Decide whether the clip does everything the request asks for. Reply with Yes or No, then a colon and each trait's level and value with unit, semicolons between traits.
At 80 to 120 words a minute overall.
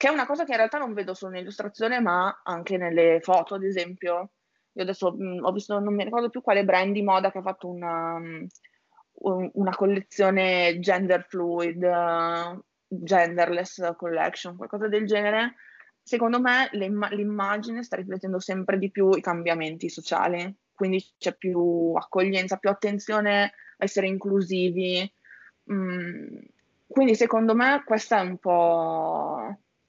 No: average, 150 wpm